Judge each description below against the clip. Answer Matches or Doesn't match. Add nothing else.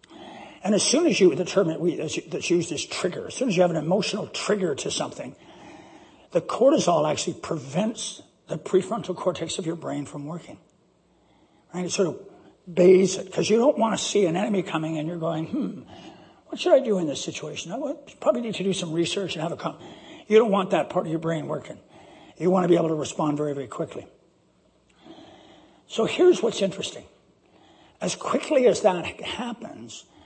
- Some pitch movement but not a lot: Matches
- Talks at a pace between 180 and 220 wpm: Matches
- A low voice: Doesn't match